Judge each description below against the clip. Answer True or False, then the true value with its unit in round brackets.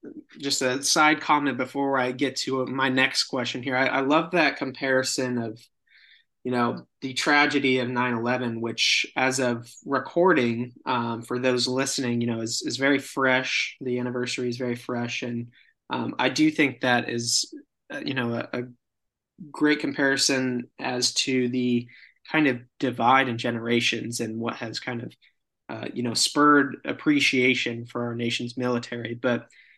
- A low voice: True (125 Hz)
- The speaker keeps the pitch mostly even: True (2.2 semitones)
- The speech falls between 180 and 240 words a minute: False (160 wpm)